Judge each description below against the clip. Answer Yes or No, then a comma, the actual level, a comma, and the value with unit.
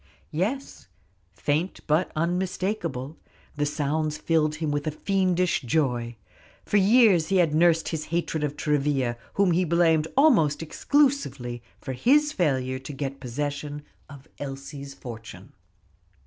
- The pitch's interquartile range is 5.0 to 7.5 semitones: No, average, 4.1 semitones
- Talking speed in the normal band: No, slow, 130 wpm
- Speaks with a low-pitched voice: No, medium, 155 Hz